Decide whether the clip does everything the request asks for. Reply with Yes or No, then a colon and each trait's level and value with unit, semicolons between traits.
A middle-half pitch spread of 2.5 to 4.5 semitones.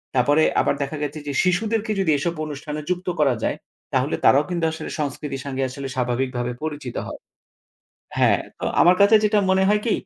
No: average, 5.1 semitones